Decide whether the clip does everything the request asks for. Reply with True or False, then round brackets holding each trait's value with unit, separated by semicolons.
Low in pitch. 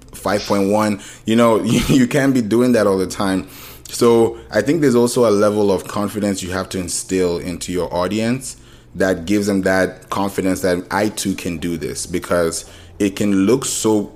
True (105 Hz)